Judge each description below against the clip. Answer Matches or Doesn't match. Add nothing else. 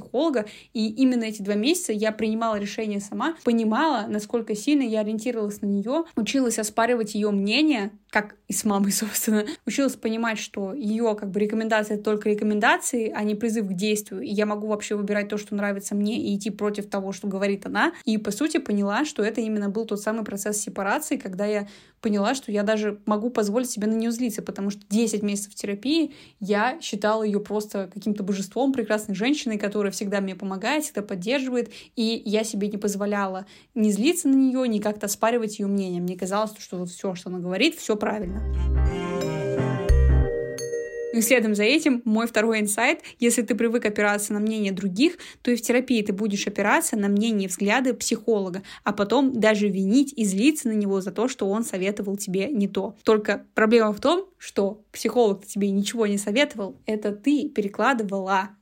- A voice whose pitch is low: Doesn't match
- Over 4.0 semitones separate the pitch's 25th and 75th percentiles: Doesn't match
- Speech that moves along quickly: Matches